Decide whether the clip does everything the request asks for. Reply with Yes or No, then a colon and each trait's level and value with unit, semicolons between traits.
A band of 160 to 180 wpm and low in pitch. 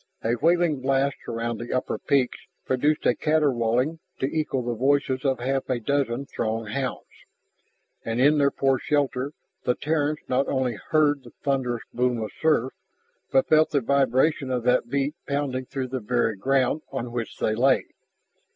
Yes: average, 165 wpm; low, 130 Hz